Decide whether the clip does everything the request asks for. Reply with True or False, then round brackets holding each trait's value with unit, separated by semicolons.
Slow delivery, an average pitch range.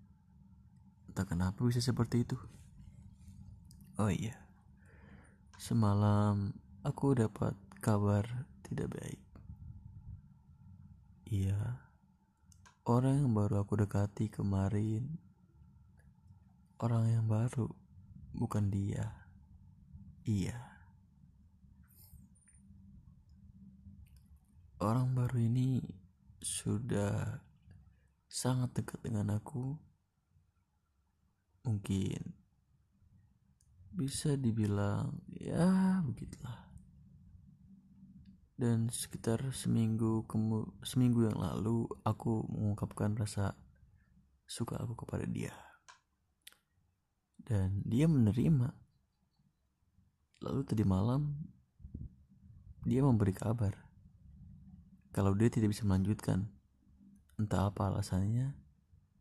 True (70 wpm; 3.9 semitones)